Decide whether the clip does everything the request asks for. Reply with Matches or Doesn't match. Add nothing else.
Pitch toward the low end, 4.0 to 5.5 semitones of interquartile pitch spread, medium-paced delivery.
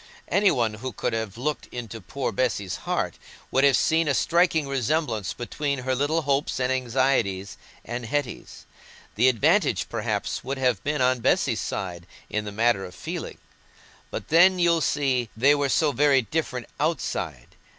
Matches